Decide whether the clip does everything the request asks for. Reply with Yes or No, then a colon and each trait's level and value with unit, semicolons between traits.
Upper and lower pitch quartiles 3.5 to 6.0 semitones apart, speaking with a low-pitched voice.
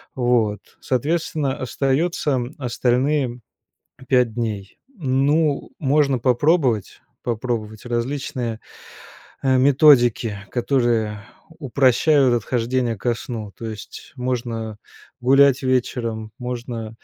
No: average, 2.9 semitones; low, 125 Hz